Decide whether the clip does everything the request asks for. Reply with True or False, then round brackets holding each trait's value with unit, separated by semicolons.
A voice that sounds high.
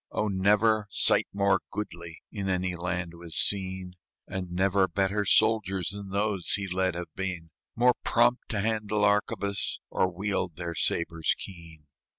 False (95 Hz)